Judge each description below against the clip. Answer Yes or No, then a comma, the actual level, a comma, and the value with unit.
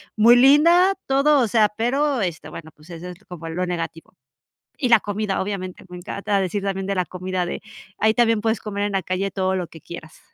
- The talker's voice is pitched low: No, high, 195 Hz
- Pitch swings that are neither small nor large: Yes, average, 4.1 semitones